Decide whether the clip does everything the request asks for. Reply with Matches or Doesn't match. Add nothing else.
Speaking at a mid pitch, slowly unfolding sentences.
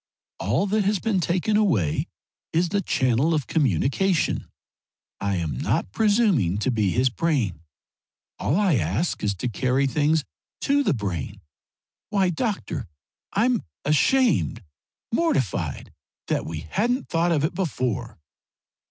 Matches